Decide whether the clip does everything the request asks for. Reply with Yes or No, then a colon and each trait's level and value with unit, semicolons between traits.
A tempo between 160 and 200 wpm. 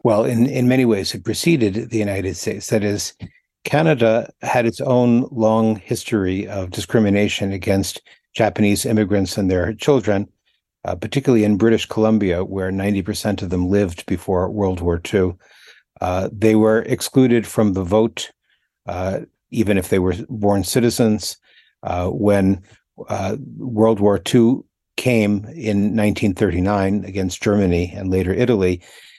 No: average, 140 wpm